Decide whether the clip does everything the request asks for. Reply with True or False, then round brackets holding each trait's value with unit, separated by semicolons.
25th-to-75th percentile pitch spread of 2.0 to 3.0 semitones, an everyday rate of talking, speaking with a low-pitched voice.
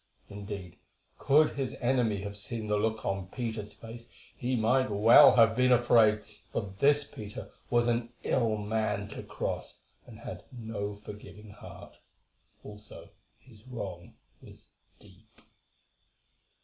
False (2.7 semitones; 130 wpm; 110 Hz)